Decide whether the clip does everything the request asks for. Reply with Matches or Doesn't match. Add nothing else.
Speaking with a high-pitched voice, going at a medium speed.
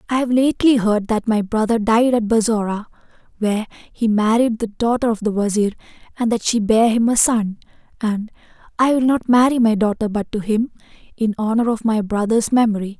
Matches